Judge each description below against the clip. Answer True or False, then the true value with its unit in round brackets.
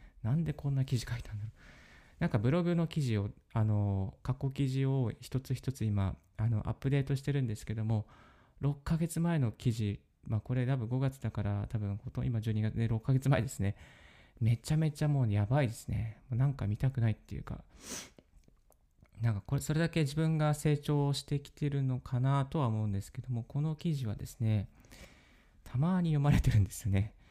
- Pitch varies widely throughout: False (4.6 semitones)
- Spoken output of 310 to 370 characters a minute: True (365 characters per minute)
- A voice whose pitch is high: False (125 Hz)